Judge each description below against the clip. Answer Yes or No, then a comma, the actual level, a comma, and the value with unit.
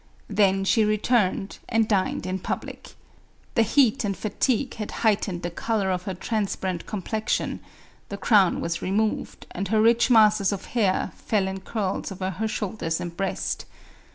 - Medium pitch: No, high, 200 Hz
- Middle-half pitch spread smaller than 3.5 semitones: Yes, average, 2.7 semitones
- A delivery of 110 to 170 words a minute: Yes, average, 160 wpm